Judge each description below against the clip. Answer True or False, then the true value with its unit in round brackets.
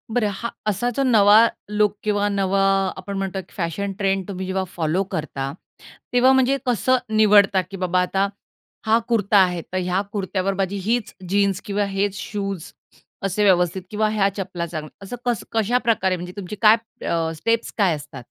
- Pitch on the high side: True (195 Hz)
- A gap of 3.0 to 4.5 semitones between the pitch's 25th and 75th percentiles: False (2.4 semitones)